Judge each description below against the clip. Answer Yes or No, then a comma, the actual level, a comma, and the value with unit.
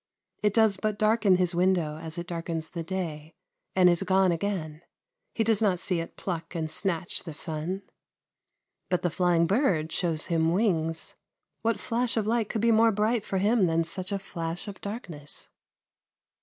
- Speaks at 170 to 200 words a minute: Yes, average, 175 wpm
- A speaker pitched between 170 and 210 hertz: Yes, medium, 185 Hz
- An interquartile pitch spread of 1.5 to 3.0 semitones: No, average, 3.9 semitones